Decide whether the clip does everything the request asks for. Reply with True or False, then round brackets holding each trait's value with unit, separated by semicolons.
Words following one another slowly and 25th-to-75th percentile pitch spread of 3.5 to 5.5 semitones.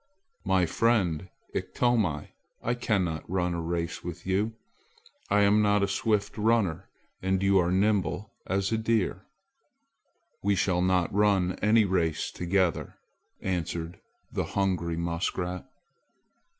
False (125 wpm; 2.8 semitones)